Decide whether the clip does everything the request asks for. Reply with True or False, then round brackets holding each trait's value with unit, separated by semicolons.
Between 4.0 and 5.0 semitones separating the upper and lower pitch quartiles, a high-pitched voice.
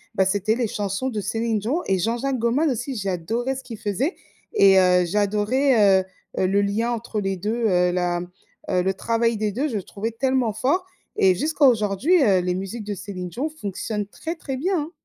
True (4.7 semitones; 215 Hz)